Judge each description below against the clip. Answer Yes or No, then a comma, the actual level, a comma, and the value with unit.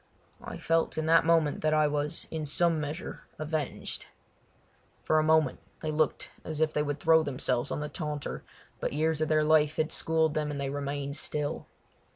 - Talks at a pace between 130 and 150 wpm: No, average, 190 wpm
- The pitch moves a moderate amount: No, narrow, 1.3 semitones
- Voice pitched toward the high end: No, medium, 155 Hz